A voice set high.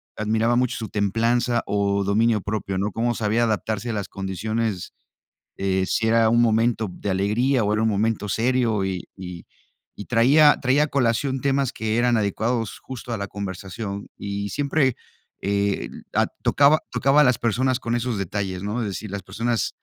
No: low, 110 Hz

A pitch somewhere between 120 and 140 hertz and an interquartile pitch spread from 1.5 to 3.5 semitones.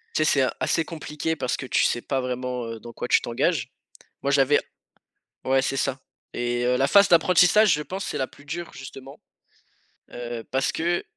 No: low, 135 Hz; average, 4.4 semitones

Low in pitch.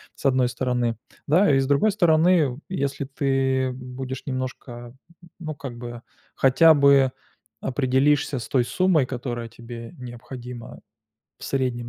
Yes: low, 130 Hz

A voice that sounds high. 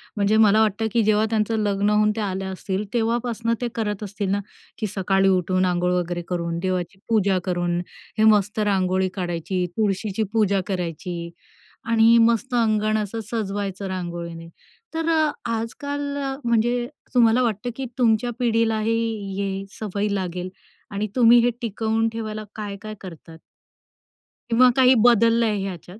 Yes: high, 210 Hz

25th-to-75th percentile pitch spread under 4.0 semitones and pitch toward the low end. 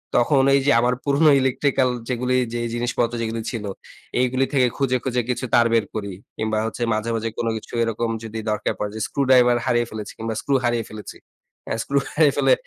Yes: narrow, 2.4 semitones; low, 120 Hz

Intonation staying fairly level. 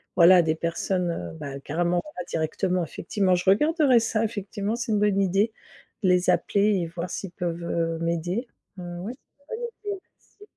No: average, 3.7 semitones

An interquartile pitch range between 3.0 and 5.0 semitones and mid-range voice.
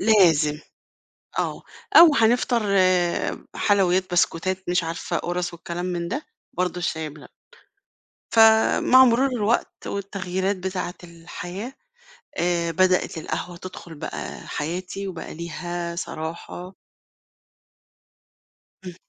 No: narrow, 2.6 semitones; medium, 180 Hz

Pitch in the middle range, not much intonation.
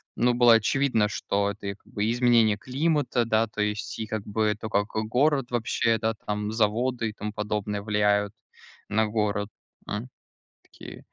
No: low, 110 Hz; narrow, 2.3 semitones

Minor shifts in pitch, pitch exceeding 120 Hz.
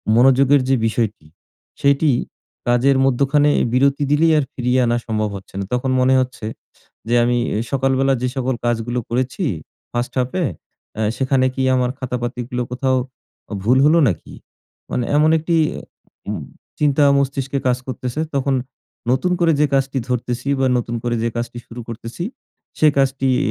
Yes: narrow, 2.3 semitones; low, 130 Hz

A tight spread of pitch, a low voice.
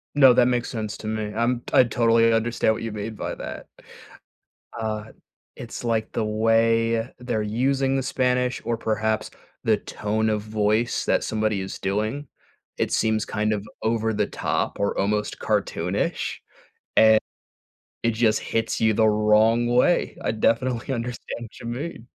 Yes: narrow, 1.8 semitones; low, 115 Hz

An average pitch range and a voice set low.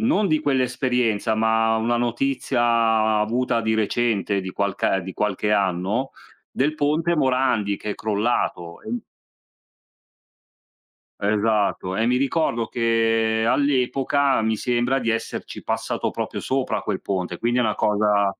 Yes: average, 3.4 semitones; low, 115 Hz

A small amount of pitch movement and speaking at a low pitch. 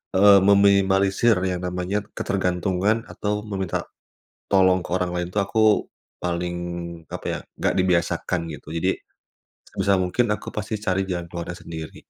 Yes: narrow, 1.9 semitones; very low, 95 Hz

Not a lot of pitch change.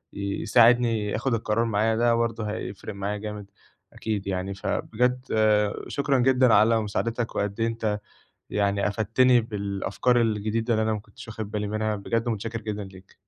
Yes: narrow, 2.0 semitones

